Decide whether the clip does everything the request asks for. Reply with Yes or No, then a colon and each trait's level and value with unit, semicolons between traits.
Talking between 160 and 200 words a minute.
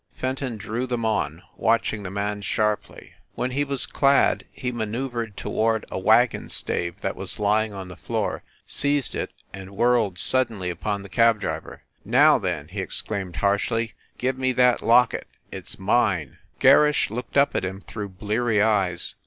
Yes: average, 170 wpm